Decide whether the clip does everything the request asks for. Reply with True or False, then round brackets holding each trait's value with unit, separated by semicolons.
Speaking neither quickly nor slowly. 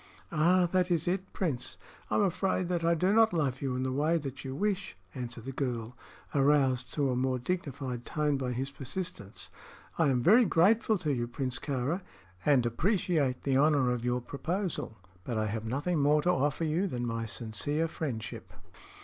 True (185 wpm)